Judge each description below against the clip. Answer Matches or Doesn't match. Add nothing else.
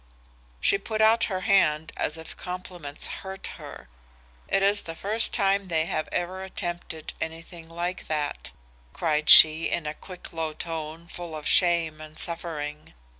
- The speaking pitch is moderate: Matches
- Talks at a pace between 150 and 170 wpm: Matches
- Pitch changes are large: Doesn't match